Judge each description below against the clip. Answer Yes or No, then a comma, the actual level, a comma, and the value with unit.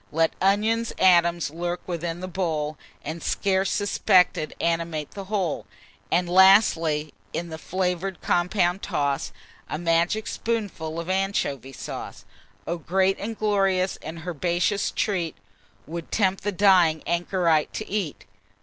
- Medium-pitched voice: Yes, medium, 175 Hz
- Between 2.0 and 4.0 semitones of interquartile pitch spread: Yes, average, 2.9 semitones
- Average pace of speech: No, slow, 130 wpm